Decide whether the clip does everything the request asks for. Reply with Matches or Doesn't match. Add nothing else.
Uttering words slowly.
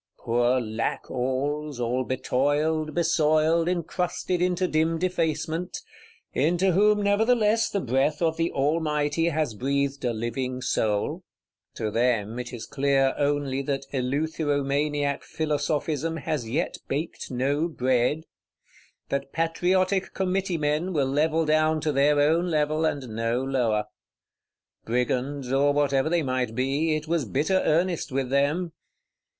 Matches